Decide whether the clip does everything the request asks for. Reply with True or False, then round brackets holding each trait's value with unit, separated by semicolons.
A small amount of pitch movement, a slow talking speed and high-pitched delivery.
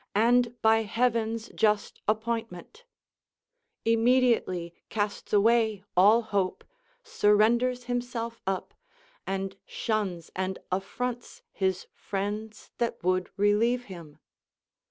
False (3.3 semitones; 100 wpm; 220 Hz)